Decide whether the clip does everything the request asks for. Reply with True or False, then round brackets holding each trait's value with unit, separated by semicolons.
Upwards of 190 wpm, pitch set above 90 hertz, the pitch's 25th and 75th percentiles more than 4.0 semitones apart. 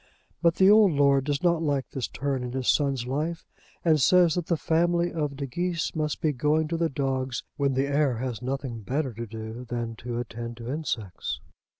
True (205 wpm; 140 Hz; 4.5 semitones)